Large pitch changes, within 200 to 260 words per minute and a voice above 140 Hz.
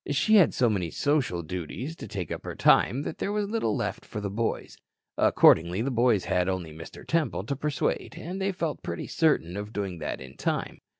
No: wide, 8.9 semitones; fast, 205 wpm; low, 115 Hz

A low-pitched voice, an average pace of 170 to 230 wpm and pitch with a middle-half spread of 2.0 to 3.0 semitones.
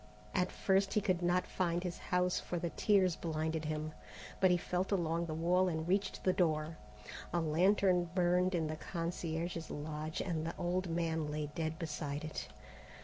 No: medium, 170 Hz; average, 175 wpm; narrow, 2.4 semitones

